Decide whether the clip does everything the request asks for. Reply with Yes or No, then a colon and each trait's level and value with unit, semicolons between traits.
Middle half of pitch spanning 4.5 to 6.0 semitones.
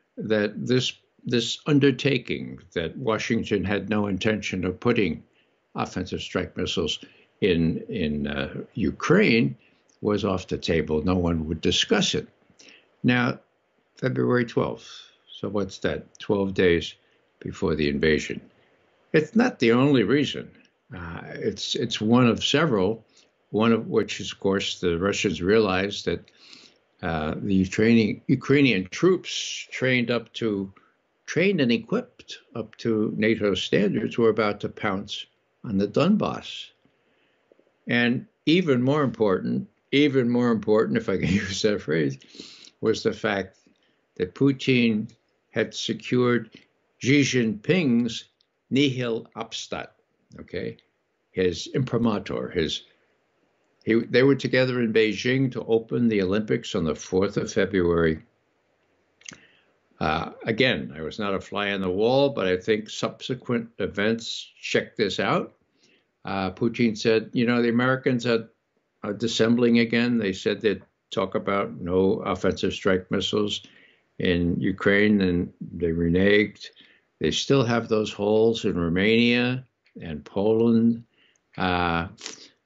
No: average, 3.8 semitones